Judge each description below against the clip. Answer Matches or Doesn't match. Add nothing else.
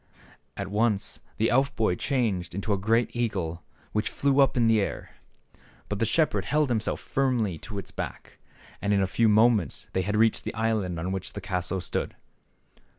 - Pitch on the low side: Matches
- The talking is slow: Doesn't match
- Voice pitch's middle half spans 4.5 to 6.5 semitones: Doesn't match